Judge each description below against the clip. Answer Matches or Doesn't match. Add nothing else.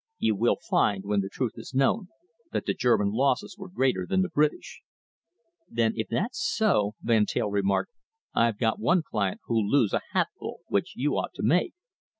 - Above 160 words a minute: Matches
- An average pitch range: Doesn't match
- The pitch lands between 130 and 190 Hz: Doesn't match